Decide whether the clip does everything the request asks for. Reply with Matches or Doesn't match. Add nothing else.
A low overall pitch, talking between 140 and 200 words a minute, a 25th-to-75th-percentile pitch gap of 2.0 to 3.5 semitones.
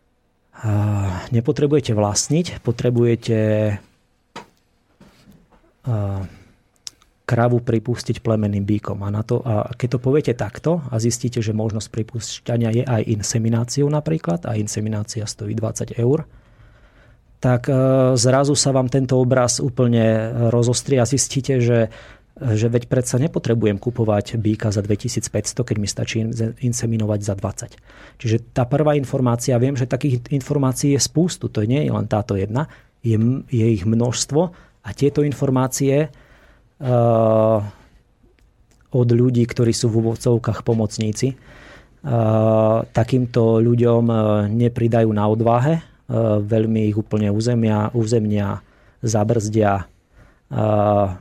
Doesn't match